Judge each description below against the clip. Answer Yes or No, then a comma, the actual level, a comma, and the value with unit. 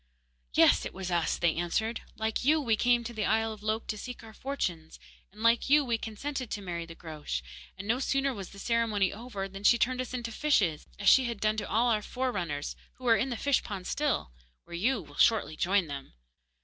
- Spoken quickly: Yes, fast, 225 wpm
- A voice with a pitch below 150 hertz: No, high, 220 Hz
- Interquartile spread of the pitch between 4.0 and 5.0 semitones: Yes, average, 4.6 semitones